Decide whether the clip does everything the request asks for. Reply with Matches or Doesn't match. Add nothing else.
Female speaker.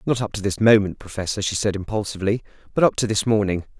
Doesn't match